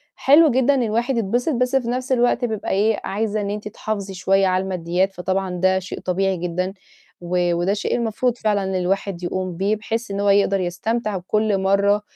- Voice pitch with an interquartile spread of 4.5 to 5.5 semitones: No, average, 3.2 semitones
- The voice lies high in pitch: Yes, high, 200 Hz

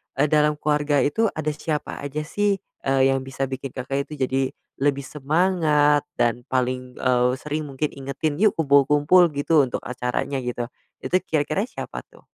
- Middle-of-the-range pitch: Yes, medium, 145 Hz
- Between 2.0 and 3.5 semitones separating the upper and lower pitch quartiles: Yes, narrow, 2.4 semitones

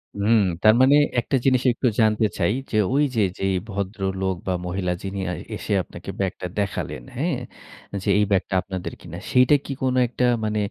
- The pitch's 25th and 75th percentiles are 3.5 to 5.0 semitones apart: Yes, average, 4.3 semitones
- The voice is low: Yes, low, 105 Hz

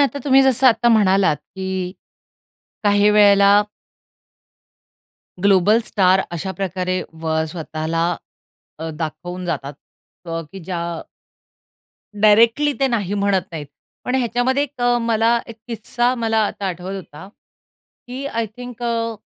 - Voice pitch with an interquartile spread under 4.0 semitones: No, average, 4.4 semitones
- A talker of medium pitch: No, high, 205 Hz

